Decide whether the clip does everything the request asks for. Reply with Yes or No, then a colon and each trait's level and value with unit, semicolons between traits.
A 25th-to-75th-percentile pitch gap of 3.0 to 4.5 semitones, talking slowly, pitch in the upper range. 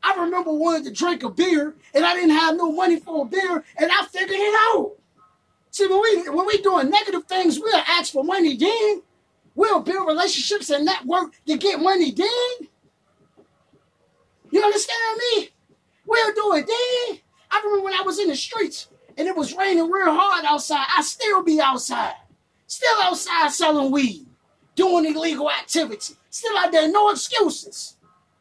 No: average, 4.1 semitones; average, 175 wpm; very high, 360 Hz